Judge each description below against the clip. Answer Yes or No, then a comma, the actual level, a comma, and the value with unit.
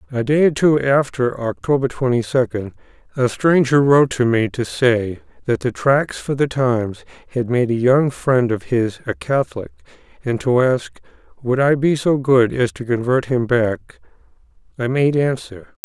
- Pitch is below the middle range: Yes, low, 125 Hz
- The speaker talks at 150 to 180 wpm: Yes, average, 175 wpm